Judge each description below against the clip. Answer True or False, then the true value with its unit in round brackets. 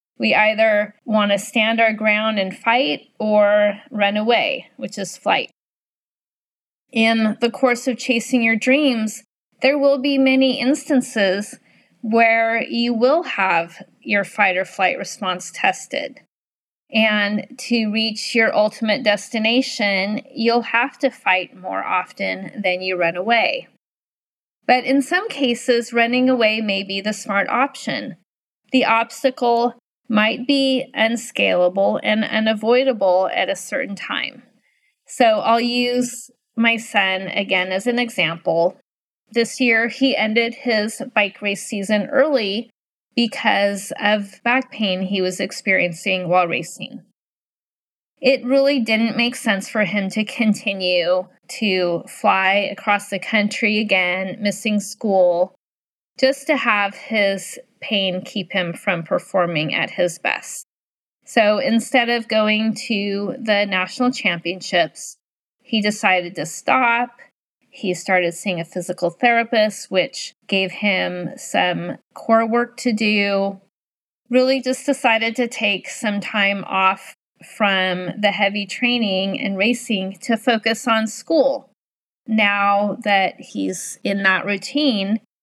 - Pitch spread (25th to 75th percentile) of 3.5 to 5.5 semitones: True (3.8 semitones)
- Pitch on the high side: True (215 Hz)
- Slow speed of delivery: True (125 wpm)